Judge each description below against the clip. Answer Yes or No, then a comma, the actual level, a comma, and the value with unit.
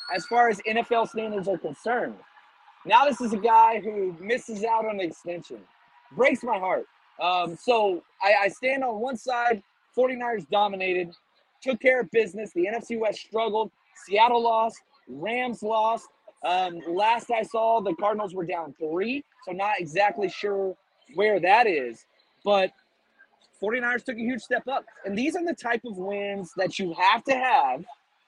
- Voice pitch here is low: No, high, 225 Hz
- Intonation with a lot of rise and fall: No, average, 3.8 semitones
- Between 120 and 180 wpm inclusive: Yes, average, 165 wpm